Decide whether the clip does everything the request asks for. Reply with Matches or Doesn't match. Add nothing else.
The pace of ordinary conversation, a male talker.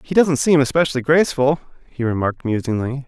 Matches